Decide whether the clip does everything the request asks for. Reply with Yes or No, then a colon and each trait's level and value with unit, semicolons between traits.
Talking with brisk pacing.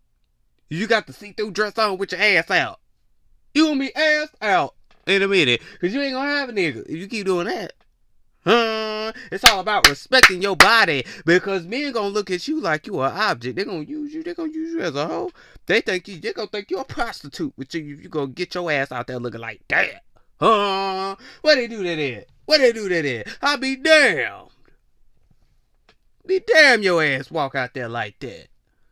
Yes: fast, 220 wpm